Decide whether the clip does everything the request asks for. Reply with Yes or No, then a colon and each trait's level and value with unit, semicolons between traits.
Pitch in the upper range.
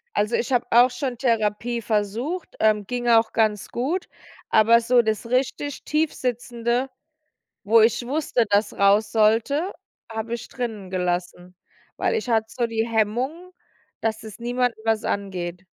Yes: high, 230 Hz